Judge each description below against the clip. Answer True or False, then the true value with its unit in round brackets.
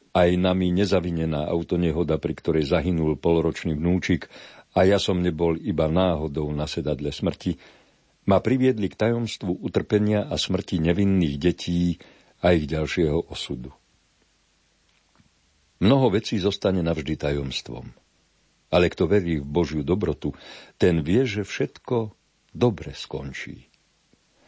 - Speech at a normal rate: True (120 wpm)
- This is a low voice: True (85 Hz)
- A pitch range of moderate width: True (3.4 semitones)